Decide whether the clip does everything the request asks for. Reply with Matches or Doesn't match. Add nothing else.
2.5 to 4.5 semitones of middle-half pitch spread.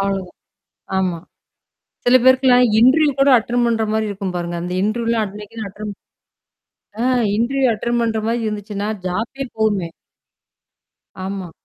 Matches